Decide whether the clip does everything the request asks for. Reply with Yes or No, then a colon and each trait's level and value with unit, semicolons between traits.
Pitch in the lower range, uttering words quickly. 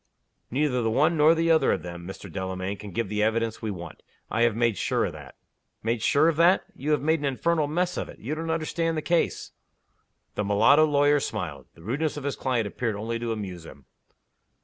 Yes: low, 120 Hz; fast, 215 wpm